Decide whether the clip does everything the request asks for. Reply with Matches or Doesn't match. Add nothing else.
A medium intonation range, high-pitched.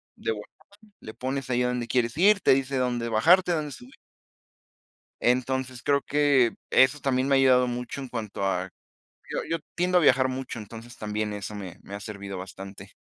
Doesn't match